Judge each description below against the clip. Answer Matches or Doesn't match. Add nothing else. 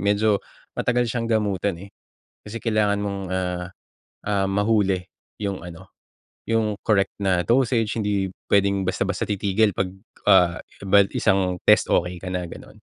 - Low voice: Matches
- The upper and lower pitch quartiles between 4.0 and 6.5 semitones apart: Doesn't match